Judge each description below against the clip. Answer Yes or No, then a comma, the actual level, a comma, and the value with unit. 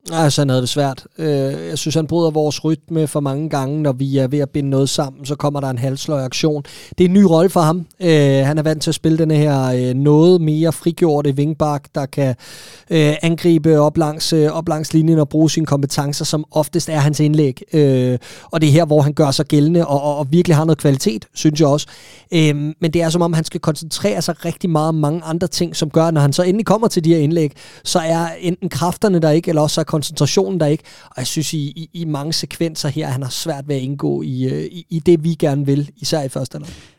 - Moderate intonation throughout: No, narrow, 2.3 semitones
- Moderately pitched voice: Yes, medium, 155 Hz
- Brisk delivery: Yes, fast, 255 wpm